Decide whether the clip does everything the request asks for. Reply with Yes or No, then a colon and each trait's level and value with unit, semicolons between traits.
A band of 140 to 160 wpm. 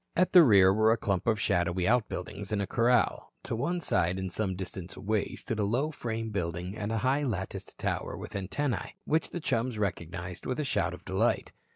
No: fast, 205 wpm